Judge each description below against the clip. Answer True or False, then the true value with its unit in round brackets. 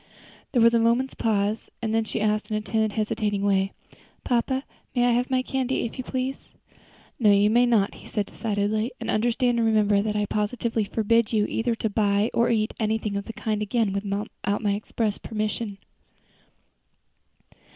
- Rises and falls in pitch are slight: True (2.1 semitones)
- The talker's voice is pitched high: True (220 Hz)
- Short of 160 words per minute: False (180 wpm)